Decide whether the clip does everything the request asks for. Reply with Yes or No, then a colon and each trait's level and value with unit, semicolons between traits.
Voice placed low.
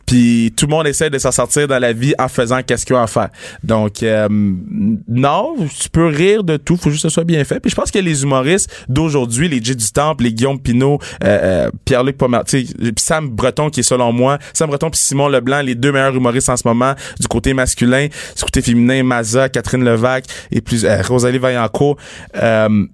Yes: low, 130 Hz